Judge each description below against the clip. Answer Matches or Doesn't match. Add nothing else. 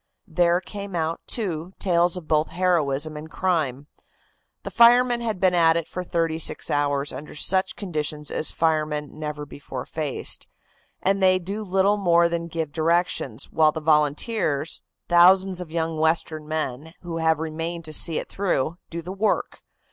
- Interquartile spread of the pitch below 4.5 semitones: Matches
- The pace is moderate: Matches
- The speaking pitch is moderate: Matches